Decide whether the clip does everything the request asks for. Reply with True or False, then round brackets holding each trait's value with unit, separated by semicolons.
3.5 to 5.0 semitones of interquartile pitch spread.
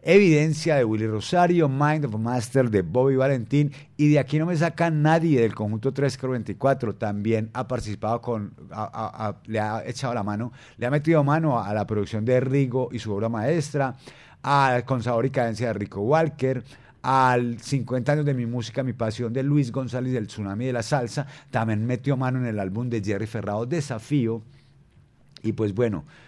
True (3.9 semitones)